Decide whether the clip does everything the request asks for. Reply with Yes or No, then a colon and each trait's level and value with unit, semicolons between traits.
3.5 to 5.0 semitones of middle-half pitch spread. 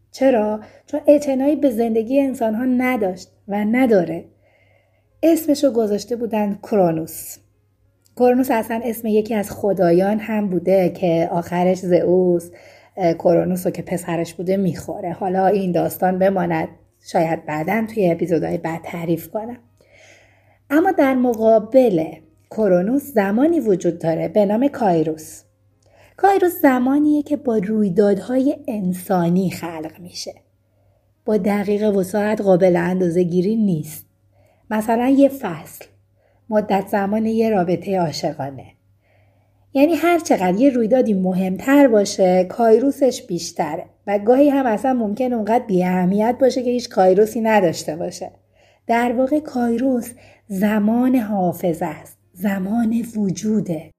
No: wide, 5.6 semitones